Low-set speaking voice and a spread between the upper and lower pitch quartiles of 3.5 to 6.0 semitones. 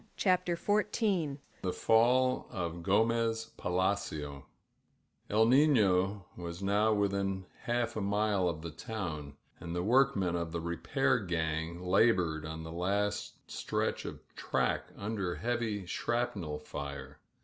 Yes: low, 100 Hz; average, 5.0 semitones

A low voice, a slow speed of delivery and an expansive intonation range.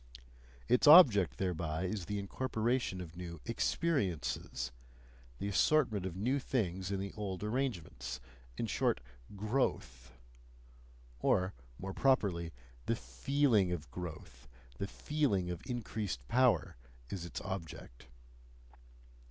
Yes: very low, 95 Hz; slow, 110 wpm; wide, 5.8 semitones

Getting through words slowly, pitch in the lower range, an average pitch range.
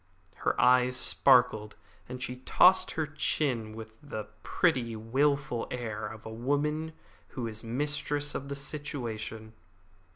Yes: slow, 130 wpm; low, 125 Hz; average, 4.5 semitones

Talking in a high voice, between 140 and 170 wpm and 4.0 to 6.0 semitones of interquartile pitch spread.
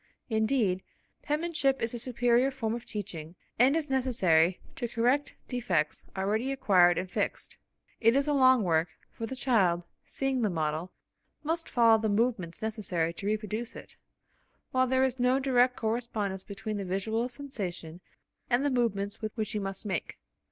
Yes: high, 225 Hz; average, 160 wpm; average, 5.1 semitones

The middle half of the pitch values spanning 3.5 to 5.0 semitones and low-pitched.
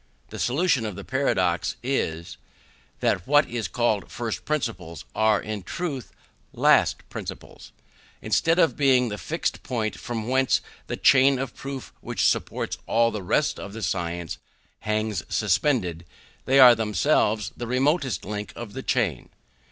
Yes: average, 4.4 semitones; low, 115 Hz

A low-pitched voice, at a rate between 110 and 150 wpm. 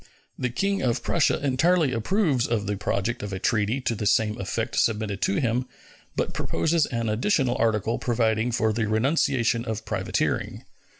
No: low, 115 Hz; average, 165 wpm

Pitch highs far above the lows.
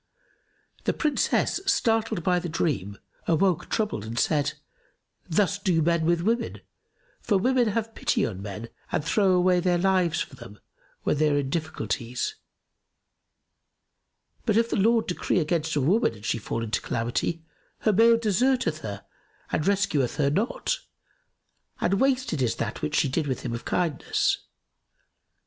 Yes: wide, 7.2 semitones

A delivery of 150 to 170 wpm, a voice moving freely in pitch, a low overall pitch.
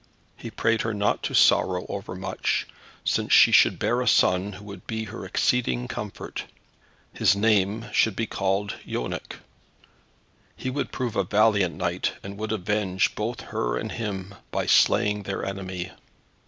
No: average, 155 wpm; average, 2.7 semitones; low, 100 Hz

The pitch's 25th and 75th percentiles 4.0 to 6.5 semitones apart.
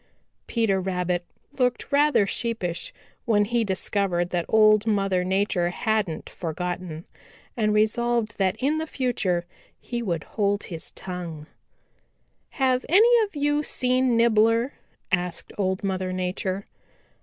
Yes: average, 4.7 semitones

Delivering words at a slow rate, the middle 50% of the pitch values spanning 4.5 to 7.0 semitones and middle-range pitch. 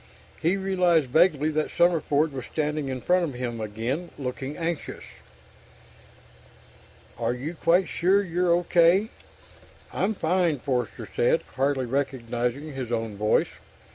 Yes: slow, 125 wpm; average, 5.3 semitones; medium, 150 Hz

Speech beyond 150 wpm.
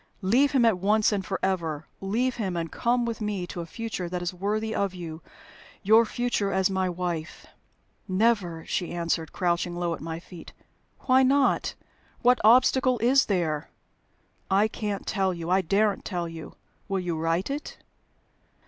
Yes: average, 165 wpm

